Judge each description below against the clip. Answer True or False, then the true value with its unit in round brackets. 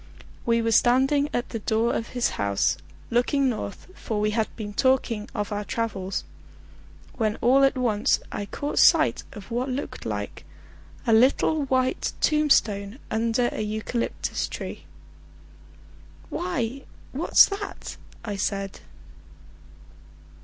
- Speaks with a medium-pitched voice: False (230 Hz)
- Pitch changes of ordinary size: True (3.7 semitones)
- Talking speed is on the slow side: True (125 wpm)